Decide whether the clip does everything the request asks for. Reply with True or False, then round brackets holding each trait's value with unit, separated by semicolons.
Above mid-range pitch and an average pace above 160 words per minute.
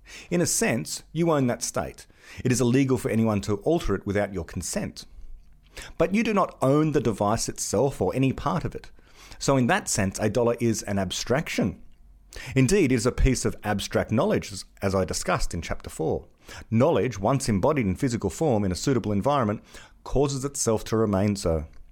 False (110 Hz; 190 wpm)